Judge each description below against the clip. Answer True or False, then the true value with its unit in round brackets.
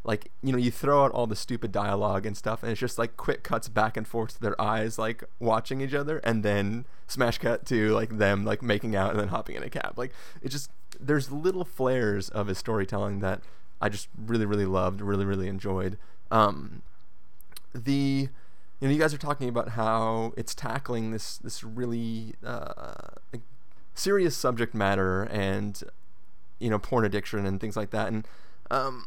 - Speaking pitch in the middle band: False (110 Hz)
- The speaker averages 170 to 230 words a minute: True (190 wpm)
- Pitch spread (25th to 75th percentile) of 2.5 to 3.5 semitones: True (3.2 semitones)